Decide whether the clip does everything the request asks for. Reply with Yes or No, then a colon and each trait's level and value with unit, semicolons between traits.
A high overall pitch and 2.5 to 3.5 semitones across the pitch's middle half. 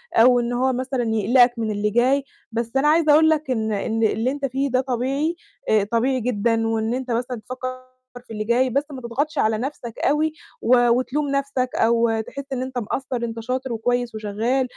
Yes: high, 245 Hz; average, 2.8 semitones